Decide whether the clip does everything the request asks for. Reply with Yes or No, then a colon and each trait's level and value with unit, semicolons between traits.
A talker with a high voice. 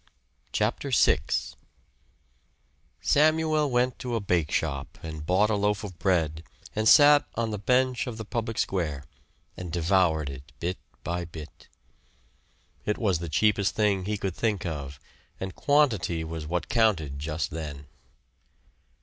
No: very low, 95 Hz